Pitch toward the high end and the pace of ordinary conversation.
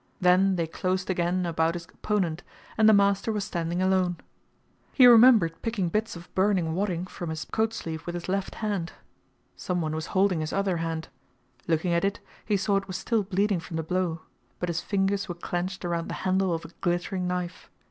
No: medium, 180 Hz; average, 195 wpm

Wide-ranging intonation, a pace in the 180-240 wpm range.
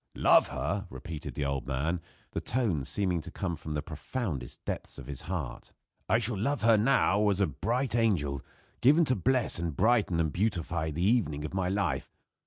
Yes: wide, 6.7 semitones; average, 190 wpm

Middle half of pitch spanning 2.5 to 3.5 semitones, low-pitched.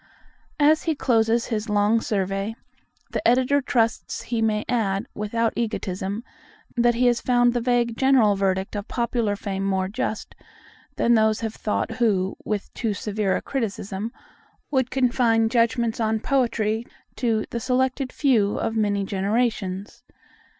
No: average, 2.8 semitones; high, 225 Hz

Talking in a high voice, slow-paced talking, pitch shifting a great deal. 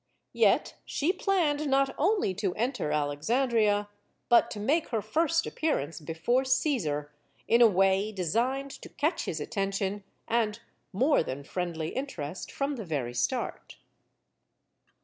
Yes: high, 215 Hz; slow, 130 wpm; wide, 7.8 semitones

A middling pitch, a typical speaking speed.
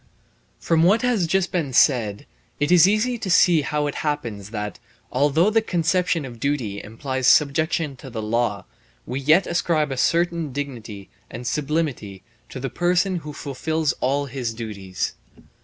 Yes: medium, 145 Hz; average, 155 wpm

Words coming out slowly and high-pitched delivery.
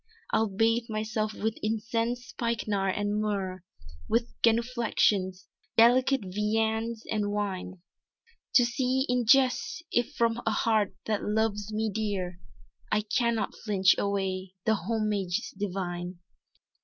Yes: slow, 120 wpm; high, 215 Hz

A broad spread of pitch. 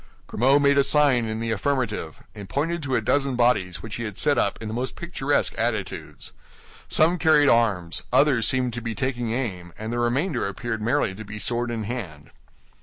No: average, 4.3 semitones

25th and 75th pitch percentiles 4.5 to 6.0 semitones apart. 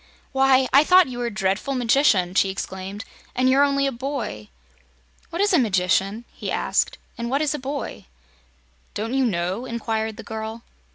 Yes: average, 4.9 semitones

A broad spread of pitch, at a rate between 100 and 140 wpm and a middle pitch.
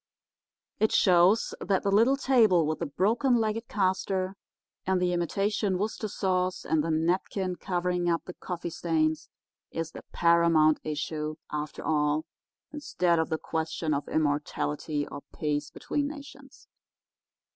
No: average, 4.0 semitones; slow, 135 wpm; medium, 175 Hz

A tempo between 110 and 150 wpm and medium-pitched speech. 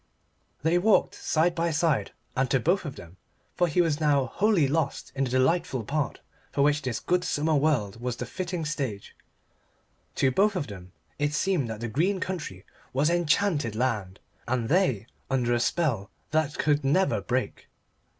No: average, 170 wpm; medium, 145 Hz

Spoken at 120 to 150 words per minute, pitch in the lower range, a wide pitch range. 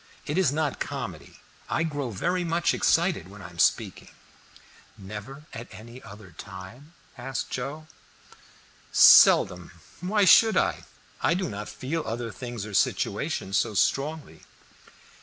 Yes: slow, 135 wpm; low, 125 Hz; wide, 7.6 semitones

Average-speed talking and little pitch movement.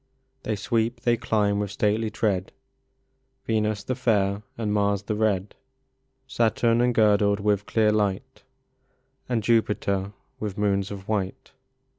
No: slow, 125 wpm; narrow, 1.7 semitones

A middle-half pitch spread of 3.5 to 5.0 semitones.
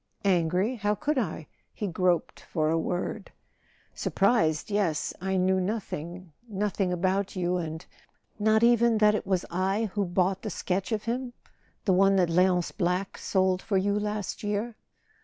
No: average, 2.7 semitones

